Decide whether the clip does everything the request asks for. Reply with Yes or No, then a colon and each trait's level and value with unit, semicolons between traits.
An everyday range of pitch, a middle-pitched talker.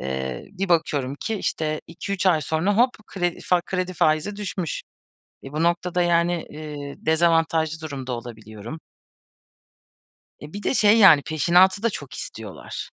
Yes: average, 4.0 semitones; medium, 165 Hz